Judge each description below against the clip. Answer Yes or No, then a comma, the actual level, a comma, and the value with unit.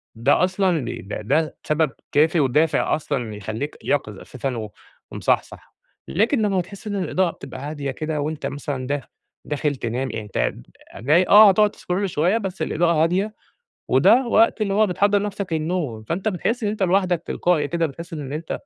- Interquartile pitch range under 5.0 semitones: No, wide, 5.4 semitones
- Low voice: No, medium, 160 Hz